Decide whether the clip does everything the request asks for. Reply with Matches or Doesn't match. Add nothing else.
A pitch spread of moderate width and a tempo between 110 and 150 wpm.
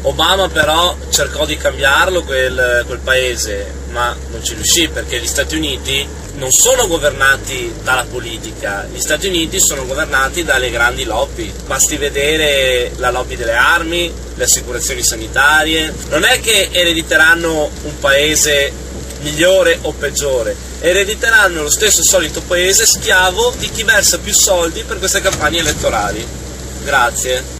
Doesn't match